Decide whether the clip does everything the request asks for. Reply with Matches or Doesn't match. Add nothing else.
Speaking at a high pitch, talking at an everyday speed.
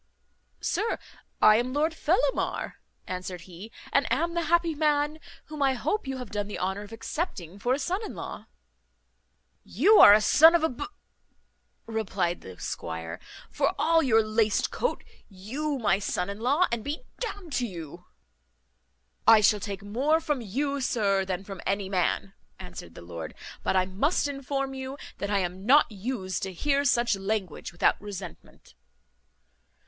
Matches